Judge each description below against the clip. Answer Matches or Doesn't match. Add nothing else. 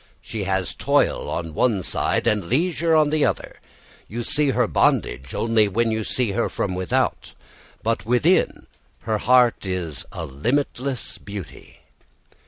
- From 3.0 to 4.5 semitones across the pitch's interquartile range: Doesn't match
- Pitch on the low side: Matches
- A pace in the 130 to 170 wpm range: Matches